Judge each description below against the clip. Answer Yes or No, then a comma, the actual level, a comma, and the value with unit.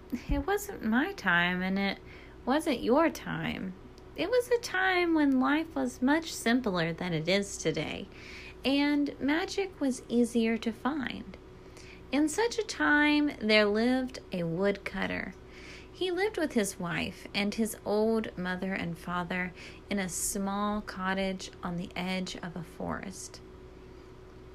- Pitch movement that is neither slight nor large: No, wide, 7.8 semitones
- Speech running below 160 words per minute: Yes, average, 140 wpm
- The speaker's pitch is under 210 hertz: No, high, 230 Hz